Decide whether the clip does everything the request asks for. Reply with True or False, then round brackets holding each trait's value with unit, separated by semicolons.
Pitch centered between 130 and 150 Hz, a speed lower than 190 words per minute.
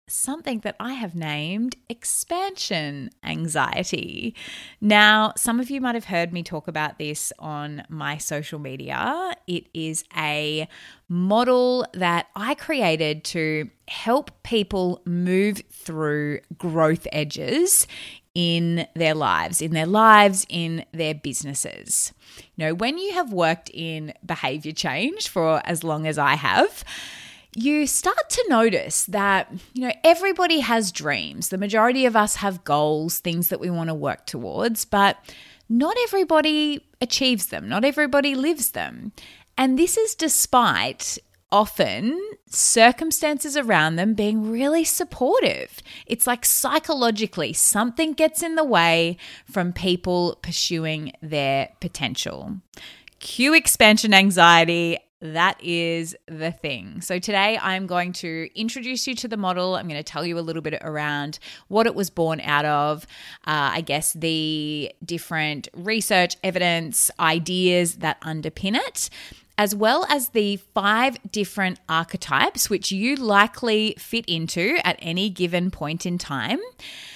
False (185 Hz; 140 wpm)